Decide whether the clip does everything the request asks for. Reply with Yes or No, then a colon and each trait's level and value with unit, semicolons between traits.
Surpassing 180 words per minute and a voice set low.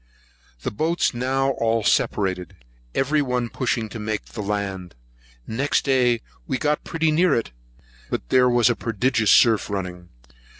No: average, 145 wpm; low, 120 Hz